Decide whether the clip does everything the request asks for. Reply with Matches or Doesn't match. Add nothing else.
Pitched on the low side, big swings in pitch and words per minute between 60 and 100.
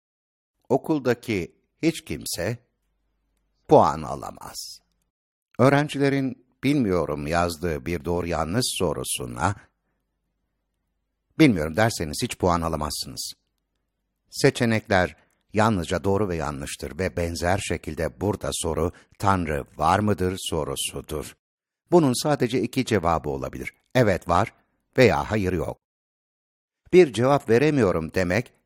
Matches